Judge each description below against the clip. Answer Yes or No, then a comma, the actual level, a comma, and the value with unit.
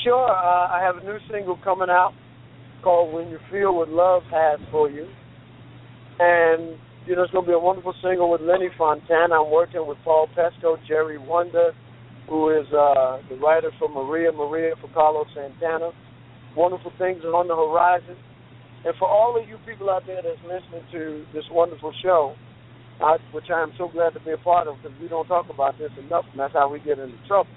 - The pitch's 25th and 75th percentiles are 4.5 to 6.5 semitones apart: No, average, 3.4 semitones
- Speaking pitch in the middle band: Yes, medium, 165 Hz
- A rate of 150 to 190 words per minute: No, fast, 205 wpm